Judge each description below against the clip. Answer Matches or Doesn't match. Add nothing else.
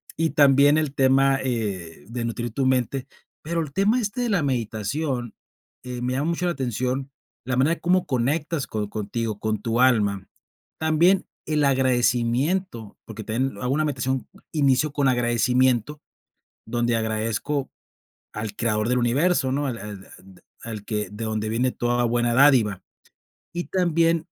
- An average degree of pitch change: Matches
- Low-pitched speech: Matches